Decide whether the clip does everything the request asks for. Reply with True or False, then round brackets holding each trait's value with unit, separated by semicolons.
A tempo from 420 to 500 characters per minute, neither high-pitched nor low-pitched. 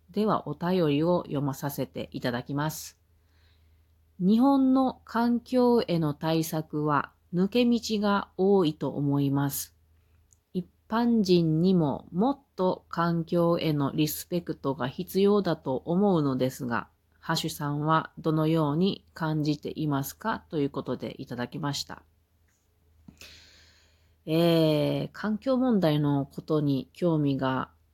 False (235 characters per minute; 150 Hz)